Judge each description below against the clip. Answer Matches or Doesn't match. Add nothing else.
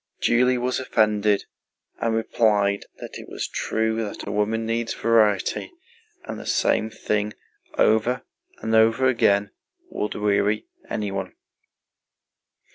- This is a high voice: Doesn't match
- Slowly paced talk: Matches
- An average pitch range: Doesn't match